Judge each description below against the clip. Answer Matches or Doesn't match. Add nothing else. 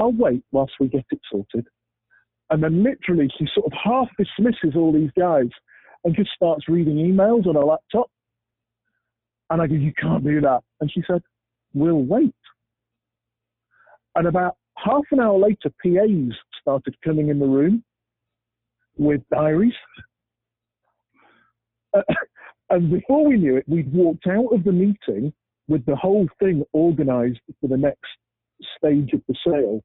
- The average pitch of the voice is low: Doesn't match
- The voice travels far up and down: Matches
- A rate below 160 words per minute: Matches